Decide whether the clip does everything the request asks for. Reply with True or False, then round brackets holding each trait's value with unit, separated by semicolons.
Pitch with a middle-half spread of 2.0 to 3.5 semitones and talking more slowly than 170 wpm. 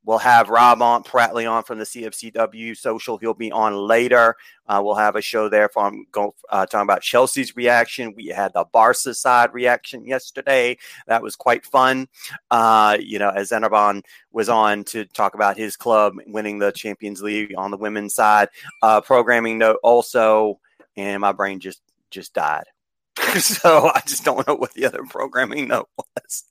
False (2.4 semitones; 180 wpm)